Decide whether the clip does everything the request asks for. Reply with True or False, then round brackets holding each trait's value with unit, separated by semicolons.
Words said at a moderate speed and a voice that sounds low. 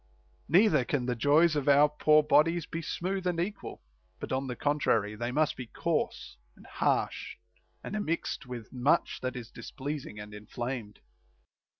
False (165 wpm; 145 Hz)